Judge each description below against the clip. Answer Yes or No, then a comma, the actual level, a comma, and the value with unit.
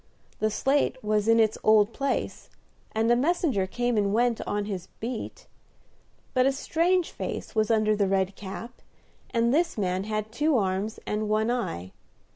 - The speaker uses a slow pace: No, average, 165 wpm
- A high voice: Yes, high, 220 Hz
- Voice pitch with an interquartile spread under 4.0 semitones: Yes, average, 3.0 semitones